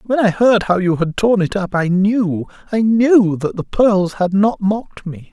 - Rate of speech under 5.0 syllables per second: Yes, 4.2 syllables/s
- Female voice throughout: No, male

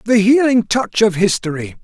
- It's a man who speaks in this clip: Yes, male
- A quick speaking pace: No, average, 165 wpm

